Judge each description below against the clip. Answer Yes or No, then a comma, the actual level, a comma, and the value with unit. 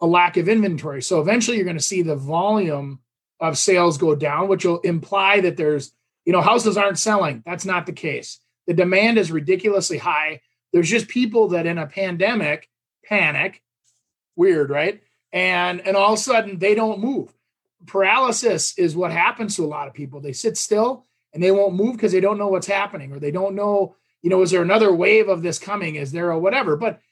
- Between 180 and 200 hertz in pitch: Yes, medium, 185 Hz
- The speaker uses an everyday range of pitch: Yes, average, 4.3 semitones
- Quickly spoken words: Yes, fast, 210 wpm